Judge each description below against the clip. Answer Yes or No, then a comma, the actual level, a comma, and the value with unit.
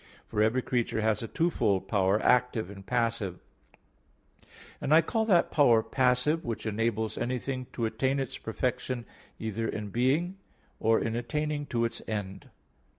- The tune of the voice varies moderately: Yes, average, 3.2 semitones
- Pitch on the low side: Yes, low, 115 Hz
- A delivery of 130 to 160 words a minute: Yes, average, 150 wpm